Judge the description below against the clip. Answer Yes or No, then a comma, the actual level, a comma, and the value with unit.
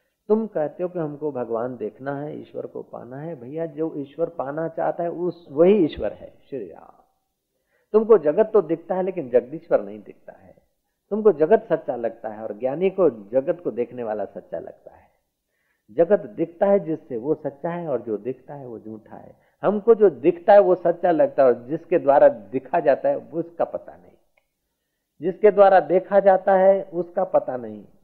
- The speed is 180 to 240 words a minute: Yes, fast, 190 wpm